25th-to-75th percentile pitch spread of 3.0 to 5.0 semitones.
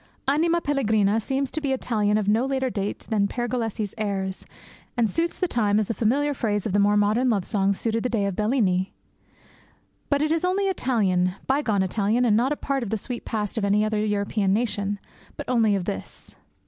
Yes: average, 4.3 semitones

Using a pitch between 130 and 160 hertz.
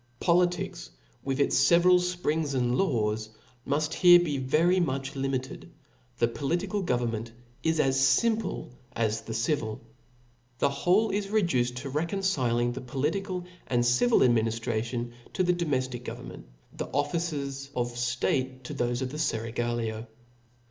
Yes: low, 135 Hz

